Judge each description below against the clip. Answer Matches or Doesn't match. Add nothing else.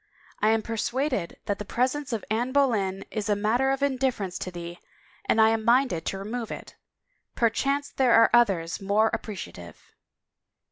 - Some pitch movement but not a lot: Matches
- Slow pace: Doesn't match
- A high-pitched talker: Matches